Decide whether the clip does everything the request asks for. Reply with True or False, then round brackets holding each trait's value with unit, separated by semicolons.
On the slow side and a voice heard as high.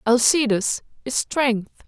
True (95 wpm; 240 Hz)